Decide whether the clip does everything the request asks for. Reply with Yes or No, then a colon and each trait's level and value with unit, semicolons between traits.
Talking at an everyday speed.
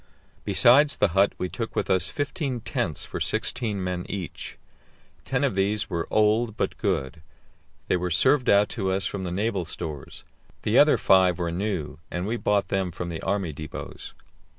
Yes: average, 175 wpm